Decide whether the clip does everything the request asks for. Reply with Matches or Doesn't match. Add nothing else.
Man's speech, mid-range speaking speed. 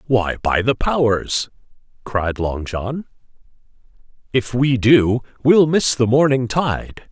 Doesn't match